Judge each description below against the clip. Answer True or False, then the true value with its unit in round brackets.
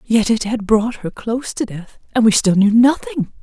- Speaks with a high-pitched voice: True (220 Hz)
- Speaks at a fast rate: True (210 wpm)